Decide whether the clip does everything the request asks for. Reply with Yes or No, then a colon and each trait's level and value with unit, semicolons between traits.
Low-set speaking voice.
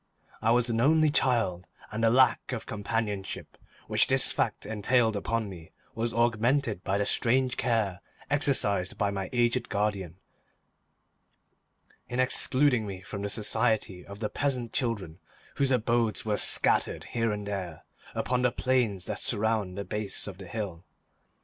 Yes: low, 110 Hz